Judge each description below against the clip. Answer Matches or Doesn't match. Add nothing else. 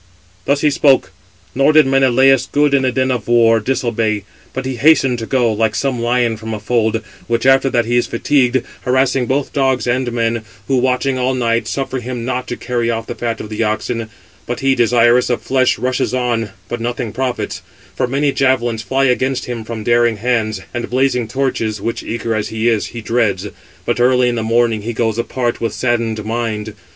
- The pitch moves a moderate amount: Doesn't match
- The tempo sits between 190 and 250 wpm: Matches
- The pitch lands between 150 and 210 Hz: Doesn't match